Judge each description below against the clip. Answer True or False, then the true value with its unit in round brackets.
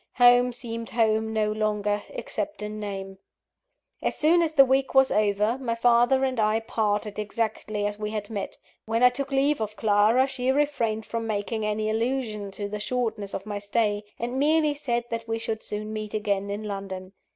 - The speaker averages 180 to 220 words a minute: True (185 wpm)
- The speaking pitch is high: True (220 Hz)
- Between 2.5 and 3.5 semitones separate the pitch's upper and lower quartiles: True (2.9 semitones)